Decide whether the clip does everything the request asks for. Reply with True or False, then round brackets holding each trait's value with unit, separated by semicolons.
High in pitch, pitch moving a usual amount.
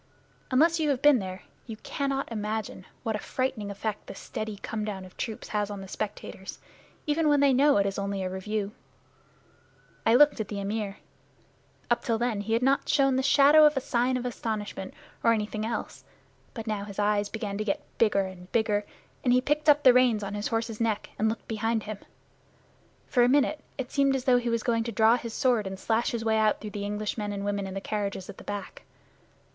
True (220 Hz; 3.7 semitones)